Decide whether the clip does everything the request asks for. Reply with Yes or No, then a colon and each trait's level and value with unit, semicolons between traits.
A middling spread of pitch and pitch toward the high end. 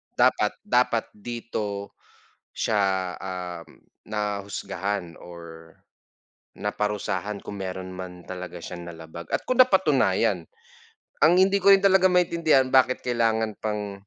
No: average, 4.7 semitones; low, 100 Hz